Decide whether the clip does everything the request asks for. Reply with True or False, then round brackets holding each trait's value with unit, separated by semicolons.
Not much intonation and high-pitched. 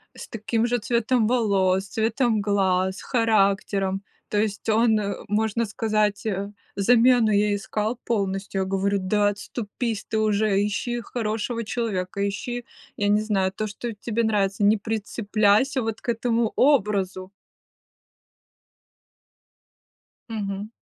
True (2.3 semitones; 210 Hz)